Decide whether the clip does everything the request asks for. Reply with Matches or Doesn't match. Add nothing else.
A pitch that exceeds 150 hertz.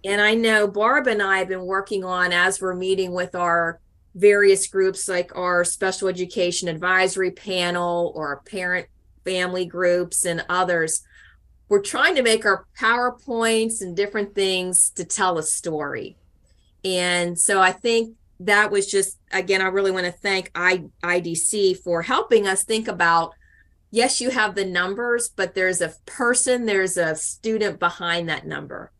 Matches